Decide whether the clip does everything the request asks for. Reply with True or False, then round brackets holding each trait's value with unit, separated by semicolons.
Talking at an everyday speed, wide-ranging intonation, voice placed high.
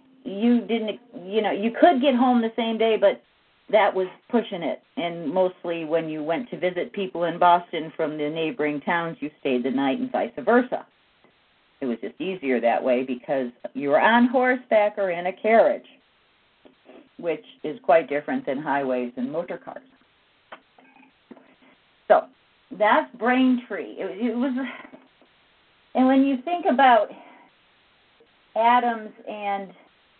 True (145 wpm; 7.6 semitones; 205 Hz)